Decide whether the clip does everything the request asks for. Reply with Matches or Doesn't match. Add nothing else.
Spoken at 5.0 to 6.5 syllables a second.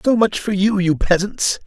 Doesn't match